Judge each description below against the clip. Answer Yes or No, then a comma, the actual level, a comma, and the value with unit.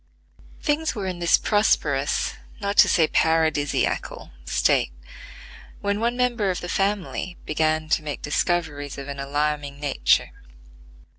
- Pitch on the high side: No, medium, 160 Hz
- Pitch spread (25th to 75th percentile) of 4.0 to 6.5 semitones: Yes, wide, 5.5 semitones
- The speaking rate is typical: No, slow, 130 wpm